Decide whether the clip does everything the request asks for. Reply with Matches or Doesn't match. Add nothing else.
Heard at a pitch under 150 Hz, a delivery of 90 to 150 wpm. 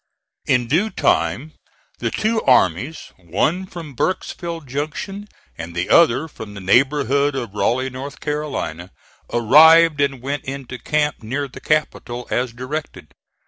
Matches